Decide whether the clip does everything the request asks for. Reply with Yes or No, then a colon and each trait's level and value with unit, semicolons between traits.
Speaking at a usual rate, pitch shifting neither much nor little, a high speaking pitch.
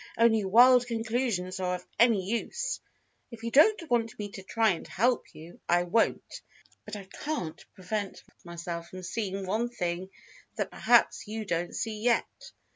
Yes: average, 160 wpm; average, 4.3 semitones; high, 215 Hz